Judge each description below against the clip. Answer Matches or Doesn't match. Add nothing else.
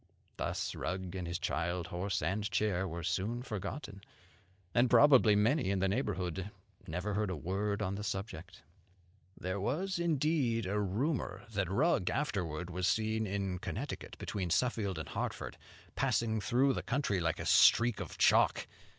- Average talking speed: Matches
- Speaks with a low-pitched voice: Matches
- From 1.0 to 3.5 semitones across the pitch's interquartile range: Doesn't match